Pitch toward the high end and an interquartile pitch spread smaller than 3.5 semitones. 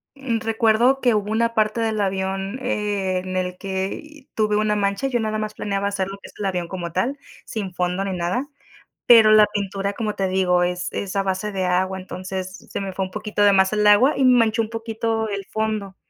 Yes: high, 205 Hz; average, 2.7 semitones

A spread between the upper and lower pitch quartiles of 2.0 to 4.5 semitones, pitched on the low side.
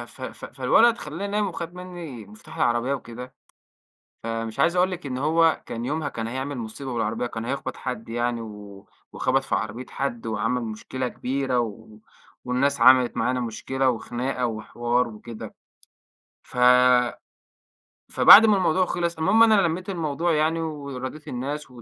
No: average, 5.1 semitones; low, 130 Hz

